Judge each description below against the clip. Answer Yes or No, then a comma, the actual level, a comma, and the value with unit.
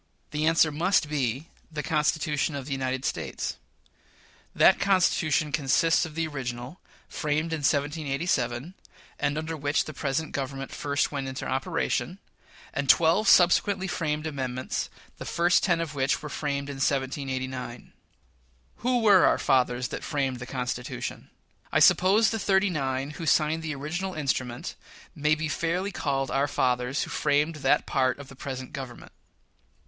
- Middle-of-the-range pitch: Yes, medium, 145 Hz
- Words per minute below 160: Yes, average, 150 wpm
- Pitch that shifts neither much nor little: Yes, average, 3.4 semitones